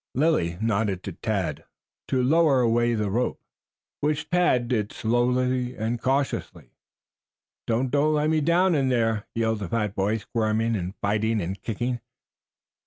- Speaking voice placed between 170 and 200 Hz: No, low, 120 Hz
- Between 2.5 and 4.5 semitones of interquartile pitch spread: Yes, average, 3.6 semitones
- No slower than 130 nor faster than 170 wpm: Yes, average, 150 wpm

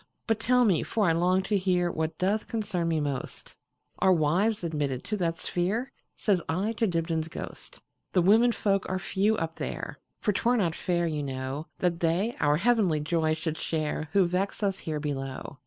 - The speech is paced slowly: No, average, 165 wpm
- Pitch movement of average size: Yes, average, 4.1 semitones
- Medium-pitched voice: Yes, medium, 175 Hz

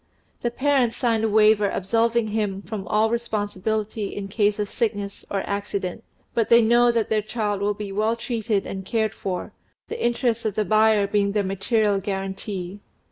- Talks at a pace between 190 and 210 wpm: No, average, 175 wpm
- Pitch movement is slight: Yes, narrow, 2.1 semitones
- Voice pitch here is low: No, high, 215 Hz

